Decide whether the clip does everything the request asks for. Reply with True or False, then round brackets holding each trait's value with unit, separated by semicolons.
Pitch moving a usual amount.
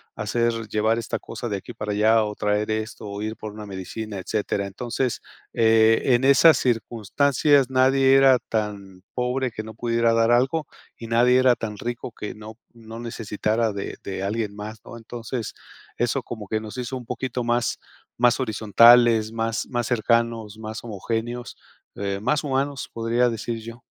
False (2.2 semitones)